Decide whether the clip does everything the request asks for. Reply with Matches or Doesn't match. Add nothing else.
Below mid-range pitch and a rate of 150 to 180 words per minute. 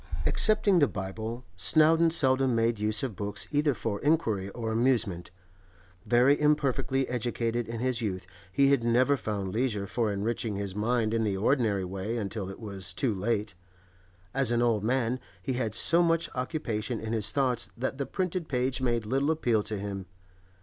Matches